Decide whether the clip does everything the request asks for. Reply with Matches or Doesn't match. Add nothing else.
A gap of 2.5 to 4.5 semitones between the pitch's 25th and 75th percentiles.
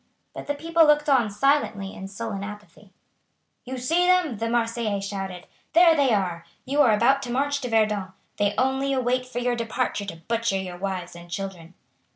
Doesn't match